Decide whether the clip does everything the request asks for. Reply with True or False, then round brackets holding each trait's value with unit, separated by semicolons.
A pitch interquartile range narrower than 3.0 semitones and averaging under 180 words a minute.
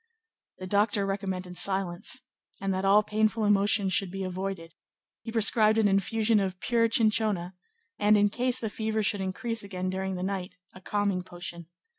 True (2.5 semitones; 165 wpm)